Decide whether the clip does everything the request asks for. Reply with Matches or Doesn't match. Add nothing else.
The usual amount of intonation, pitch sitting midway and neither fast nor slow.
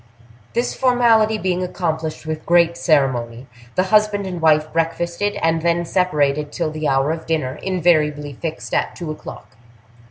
Matches